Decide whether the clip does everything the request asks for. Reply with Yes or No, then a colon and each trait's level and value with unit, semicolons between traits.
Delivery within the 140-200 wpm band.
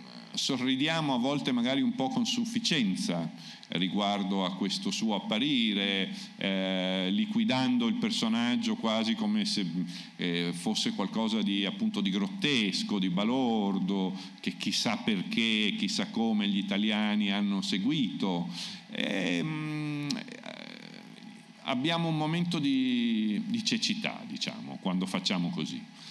No: slow, 115 wpm